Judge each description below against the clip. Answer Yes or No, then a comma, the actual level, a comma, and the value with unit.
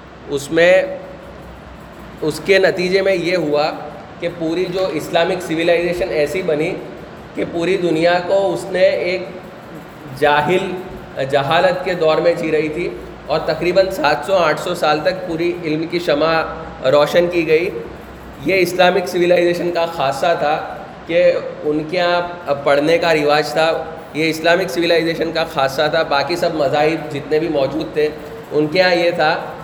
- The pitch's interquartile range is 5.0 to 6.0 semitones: No, average, 2.9 semitones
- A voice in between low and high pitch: Yes, medium, 170 Hz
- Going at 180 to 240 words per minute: No, average, 160 wpm